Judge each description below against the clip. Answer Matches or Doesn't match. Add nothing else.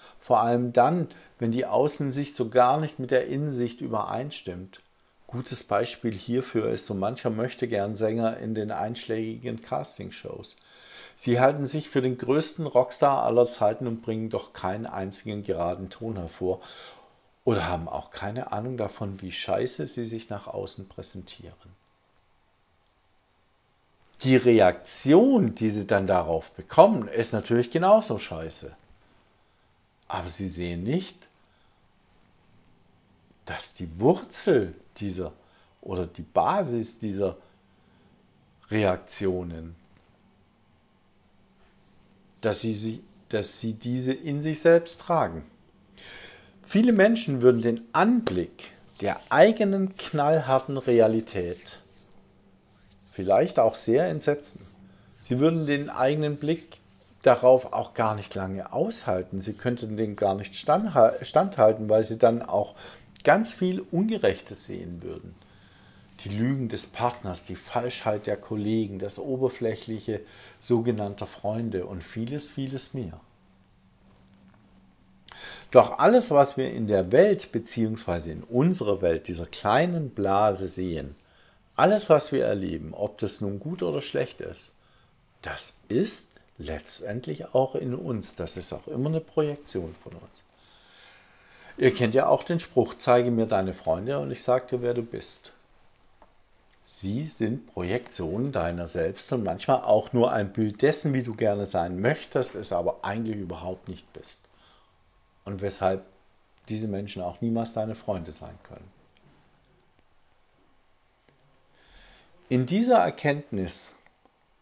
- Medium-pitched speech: Doesn't match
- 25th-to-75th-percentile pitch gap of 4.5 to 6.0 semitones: Matches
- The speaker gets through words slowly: Matches